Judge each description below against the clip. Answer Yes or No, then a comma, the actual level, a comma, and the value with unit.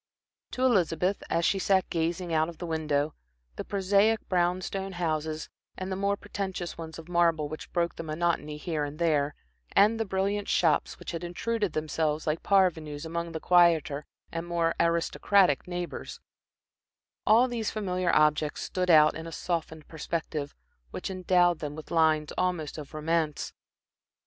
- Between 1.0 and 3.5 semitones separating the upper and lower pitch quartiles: Yes, average, 2.9 semitones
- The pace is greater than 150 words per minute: Yes, average, 160 wpm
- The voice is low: No, medium, 170 Hz